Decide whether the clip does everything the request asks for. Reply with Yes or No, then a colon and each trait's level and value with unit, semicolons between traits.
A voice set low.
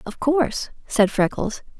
No: high, 245 Hz